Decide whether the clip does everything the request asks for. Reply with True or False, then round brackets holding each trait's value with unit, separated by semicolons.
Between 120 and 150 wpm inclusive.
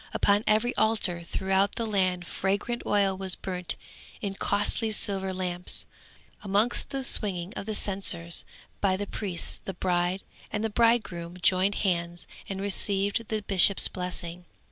True (135 wpm)